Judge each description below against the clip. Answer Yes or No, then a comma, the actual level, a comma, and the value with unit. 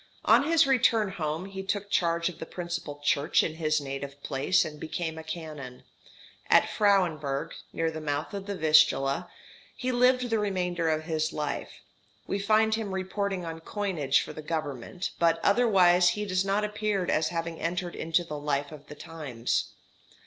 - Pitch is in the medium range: Yes, medium, 170 Hz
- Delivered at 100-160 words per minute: No, average, 170 wpm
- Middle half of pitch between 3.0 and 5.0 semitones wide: Yes, average, 4.3 semitones